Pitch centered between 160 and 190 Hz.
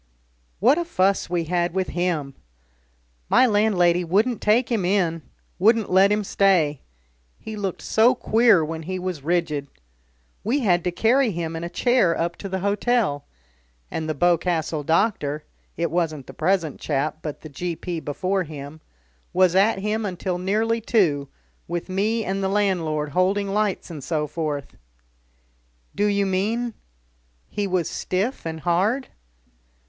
Yes: medium, 185 Hz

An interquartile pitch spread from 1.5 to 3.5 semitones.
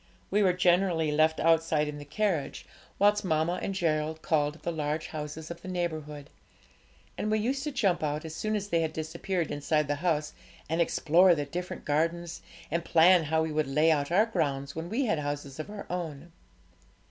Yes: average, 3.0 semitones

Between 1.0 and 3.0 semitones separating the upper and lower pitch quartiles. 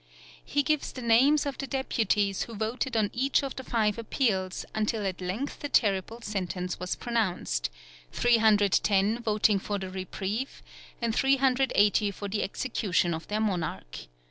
No: average, 4.3 semitones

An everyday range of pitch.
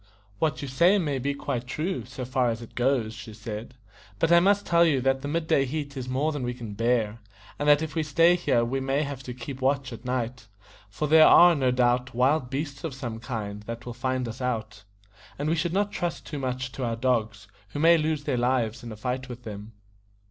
Yes: average, 3.7 semitones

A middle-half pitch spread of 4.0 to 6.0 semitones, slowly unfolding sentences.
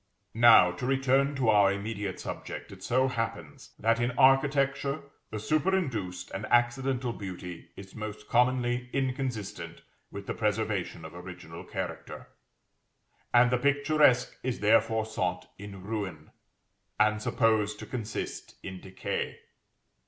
Yes: average, 4.6 semitones; slow, 125 wpm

